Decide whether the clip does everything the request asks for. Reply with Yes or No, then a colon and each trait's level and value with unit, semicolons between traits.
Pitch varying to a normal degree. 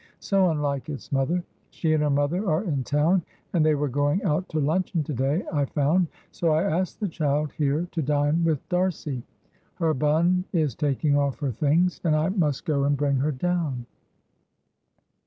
Yes: average, 3.2 semitones